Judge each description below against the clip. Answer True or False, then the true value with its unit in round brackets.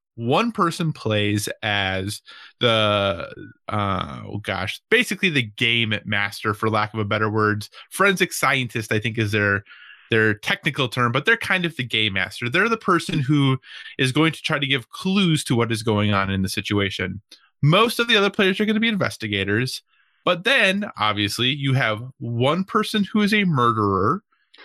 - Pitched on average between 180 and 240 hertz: False (120 Hz)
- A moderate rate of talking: True (180 wpm)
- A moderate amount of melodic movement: False (8.4 semitones)